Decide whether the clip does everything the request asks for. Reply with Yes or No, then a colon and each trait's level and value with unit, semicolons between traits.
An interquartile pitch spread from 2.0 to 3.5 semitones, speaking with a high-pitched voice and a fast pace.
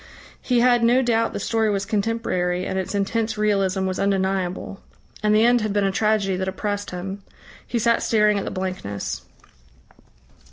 No: average, 2.9 semitones; high, 205 Hz; average, 170 wpm